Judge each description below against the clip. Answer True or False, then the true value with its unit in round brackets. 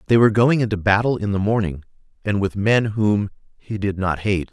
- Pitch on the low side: True (105 Hz)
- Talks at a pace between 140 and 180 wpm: False (200 wpm)